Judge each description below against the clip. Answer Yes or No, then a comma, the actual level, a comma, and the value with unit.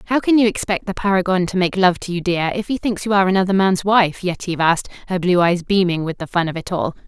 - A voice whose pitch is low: No, medium, 185 Hz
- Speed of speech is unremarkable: No, fast, 270 wpm